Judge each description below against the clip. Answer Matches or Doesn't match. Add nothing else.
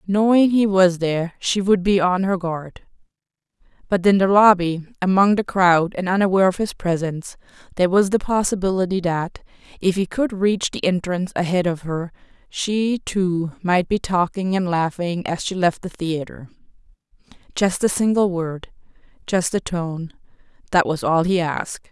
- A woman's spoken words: Matches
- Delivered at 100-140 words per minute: Doesn't match